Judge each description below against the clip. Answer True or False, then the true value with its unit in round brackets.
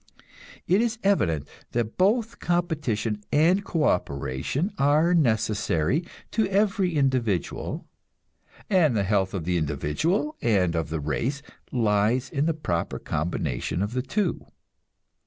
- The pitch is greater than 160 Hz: False (125 Hz)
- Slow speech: True (125 wpm)